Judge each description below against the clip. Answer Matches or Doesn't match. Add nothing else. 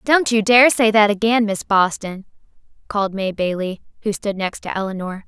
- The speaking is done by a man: Doesn't match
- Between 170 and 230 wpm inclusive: Matches